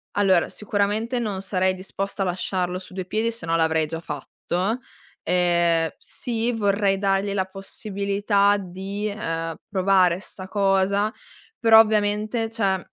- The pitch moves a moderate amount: No, narrow, 2.2 semitones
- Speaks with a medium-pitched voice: No, high, 195 Hz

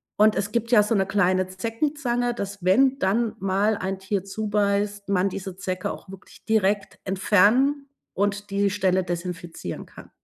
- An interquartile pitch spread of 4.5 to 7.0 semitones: No, narrow, 2.5 semitones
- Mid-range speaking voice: No, high, 200 Hz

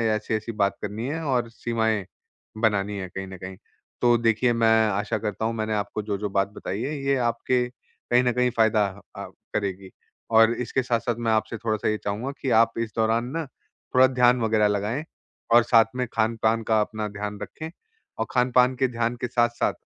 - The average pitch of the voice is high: No, low, 115 Hz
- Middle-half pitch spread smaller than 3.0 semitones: Yes, narrow, 2.4 semitones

